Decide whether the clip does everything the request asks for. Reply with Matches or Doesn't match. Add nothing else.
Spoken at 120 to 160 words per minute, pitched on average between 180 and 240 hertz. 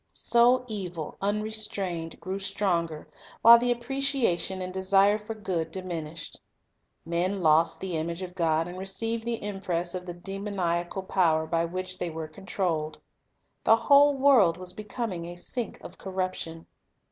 Matches